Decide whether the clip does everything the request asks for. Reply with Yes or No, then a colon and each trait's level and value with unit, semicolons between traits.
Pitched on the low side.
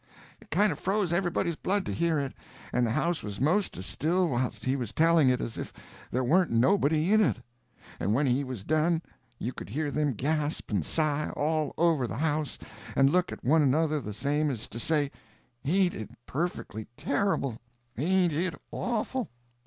No: medium, 150 Hz